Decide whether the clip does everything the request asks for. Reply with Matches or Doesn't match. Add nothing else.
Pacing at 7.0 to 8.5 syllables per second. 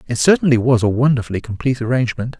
Matches